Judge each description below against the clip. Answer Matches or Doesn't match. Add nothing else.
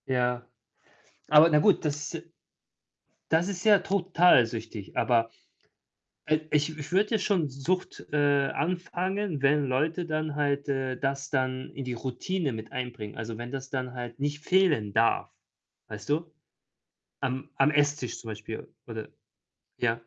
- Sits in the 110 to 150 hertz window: Matches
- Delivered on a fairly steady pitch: Doesn't match